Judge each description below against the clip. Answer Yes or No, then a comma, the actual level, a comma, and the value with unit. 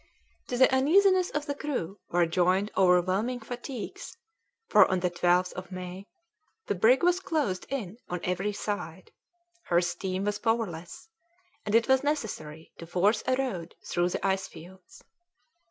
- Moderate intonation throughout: No, wide, 6.1 semitones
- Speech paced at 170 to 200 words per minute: No, average, 155 wpm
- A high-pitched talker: Yes, high, 195 Hz